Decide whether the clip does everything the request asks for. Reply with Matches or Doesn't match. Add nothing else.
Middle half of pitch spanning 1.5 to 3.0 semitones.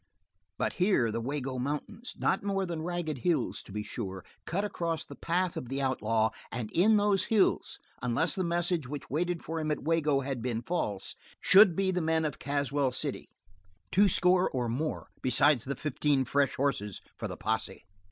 Doesn't match